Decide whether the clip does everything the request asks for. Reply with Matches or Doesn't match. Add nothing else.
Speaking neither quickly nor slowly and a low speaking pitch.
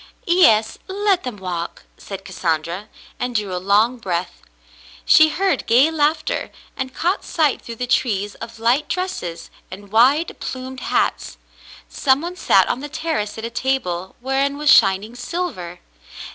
Doesn't match